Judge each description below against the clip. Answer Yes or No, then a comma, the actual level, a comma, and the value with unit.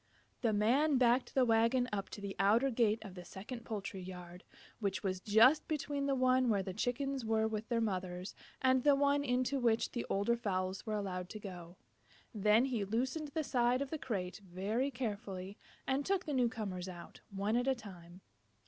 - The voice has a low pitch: No, high, 225 Hz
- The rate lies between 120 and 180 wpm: No, average, 195 wpm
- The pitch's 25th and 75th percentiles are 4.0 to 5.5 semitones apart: Yes, average, 4.9 semitones